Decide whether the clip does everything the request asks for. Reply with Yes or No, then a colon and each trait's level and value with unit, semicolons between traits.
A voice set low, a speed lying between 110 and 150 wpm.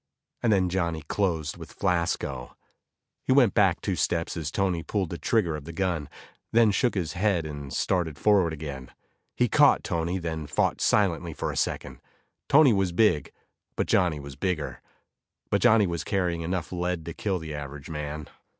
No: very low, 85 Hz; average, 175 wpm